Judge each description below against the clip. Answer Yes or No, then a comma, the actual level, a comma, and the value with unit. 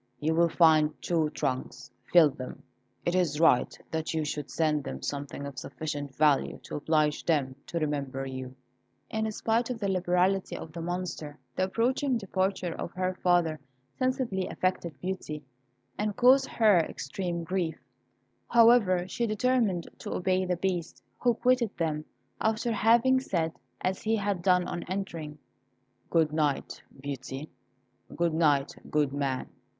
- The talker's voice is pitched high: No, medium, 175 Hz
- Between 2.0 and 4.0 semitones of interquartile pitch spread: No, average, 4.5 semitones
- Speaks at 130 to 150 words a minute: Yes, average, 145 wpm